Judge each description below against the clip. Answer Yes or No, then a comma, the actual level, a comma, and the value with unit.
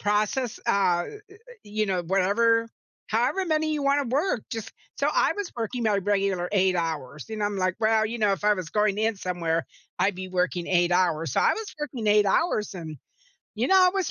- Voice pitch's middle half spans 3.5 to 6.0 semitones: Yes, average, 4.1 semitones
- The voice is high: Yes, high, 205 Hz